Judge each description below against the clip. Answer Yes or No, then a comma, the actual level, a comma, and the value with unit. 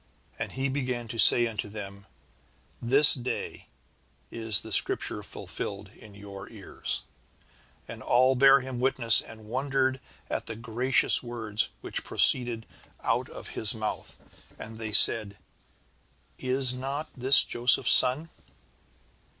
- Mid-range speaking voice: No, low, 120 Hz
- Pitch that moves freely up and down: No, average, 3.1 semitones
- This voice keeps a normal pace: No, slow, 125 wpm